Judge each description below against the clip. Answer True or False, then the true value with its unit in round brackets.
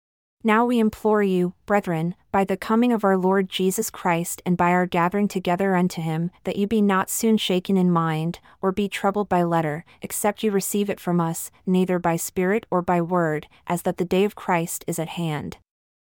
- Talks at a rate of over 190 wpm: True (200 wpm)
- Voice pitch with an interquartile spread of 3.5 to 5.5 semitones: False (2.8 semitones)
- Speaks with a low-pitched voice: False (185 Hz)